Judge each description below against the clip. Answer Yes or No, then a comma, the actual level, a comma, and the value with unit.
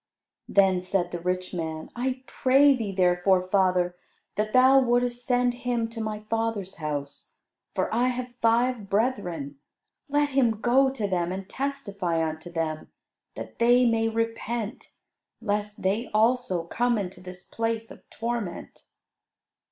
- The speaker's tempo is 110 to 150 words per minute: Yes, average, 140 wpm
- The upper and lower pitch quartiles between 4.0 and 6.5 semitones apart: Yes, average, 5.1 semitones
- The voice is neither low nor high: No, high, 220 Hz